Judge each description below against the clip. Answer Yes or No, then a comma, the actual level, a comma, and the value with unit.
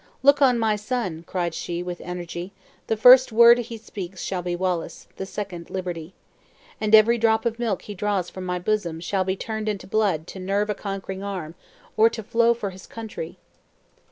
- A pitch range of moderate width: Yes, average, 3.7 semitones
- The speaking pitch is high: Yes, high, 200 Hz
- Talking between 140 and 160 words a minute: No, average, 190 wpm